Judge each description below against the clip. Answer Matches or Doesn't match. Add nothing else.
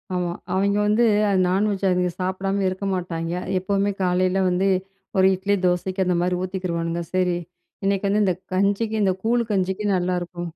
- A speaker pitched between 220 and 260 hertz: Doesn't match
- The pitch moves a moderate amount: Doesn't match